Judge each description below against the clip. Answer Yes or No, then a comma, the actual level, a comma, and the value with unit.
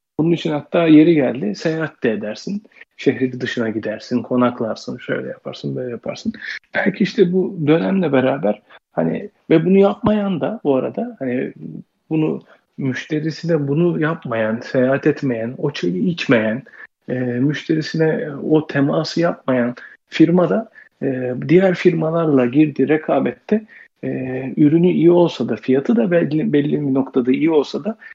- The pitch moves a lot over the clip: No, average, 5.0 semitones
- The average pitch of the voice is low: No, medium, 155 Hz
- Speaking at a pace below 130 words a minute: No, average, 135 wpm